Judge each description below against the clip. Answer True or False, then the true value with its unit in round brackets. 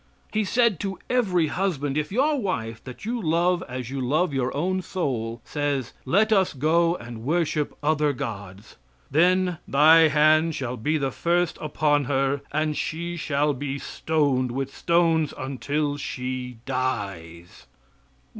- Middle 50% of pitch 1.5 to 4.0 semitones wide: False (4.8 semitones)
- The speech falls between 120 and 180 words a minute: True (140 wpm)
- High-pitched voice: False (150 Hz)